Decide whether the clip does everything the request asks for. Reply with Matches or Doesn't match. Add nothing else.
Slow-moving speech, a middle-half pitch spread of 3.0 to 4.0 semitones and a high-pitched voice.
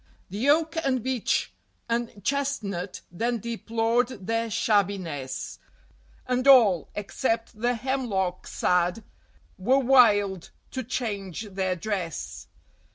Doesn't match